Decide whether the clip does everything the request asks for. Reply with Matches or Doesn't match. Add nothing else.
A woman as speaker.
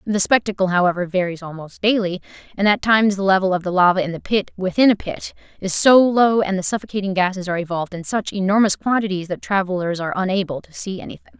Matches